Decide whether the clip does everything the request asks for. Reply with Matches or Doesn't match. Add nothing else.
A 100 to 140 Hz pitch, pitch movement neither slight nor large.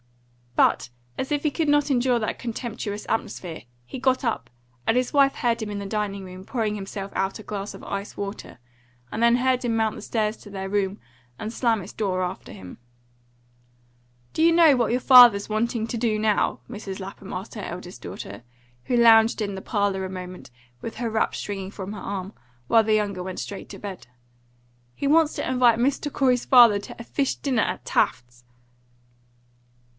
Doesn't match